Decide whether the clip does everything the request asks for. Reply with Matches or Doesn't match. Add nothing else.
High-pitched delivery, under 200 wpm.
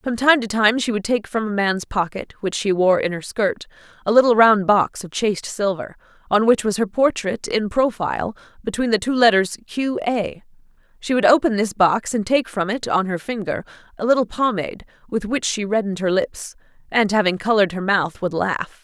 Doesn't match